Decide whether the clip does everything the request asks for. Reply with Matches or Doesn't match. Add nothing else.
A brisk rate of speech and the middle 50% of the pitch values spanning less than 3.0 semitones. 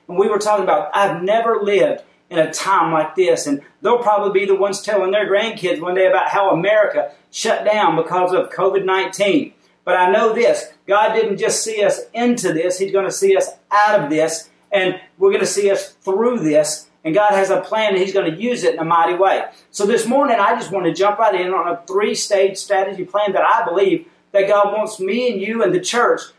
Matches